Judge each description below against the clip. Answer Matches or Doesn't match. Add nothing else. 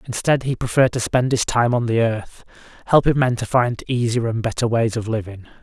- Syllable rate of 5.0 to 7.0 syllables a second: Matches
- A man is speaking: Matches